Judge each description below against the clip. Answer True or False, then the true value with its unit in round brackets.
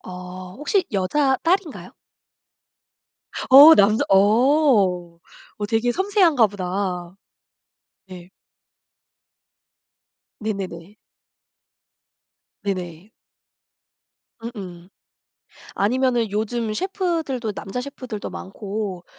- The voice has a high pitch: True (215 Hz)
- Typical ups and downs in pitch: False (6.0 semitones)